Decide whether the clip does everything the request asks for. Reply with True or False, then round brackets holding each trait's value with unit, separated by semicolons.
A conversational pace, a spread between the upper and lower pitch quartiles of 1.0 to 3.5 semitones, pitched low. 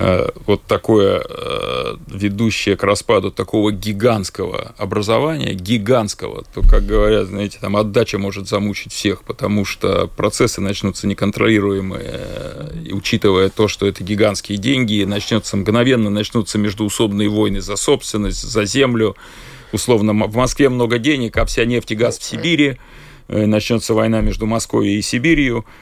True (130 wpm; 2.8 semitones; 105 Hz)